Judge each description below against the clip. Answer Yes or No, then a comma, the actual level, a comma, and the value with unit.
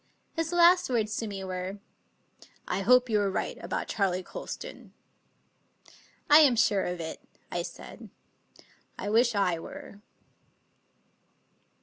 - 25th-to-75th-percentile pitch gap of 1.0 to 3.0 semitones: No, average, 4.8 semitones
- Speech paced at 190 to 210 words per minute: No, average, 140 wpm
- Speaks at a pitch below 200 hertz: No, high, 210 Hz